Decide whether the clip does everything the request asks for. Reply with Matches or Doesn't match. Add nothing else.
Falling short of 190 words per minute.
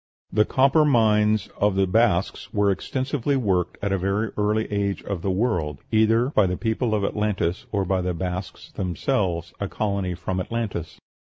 Matches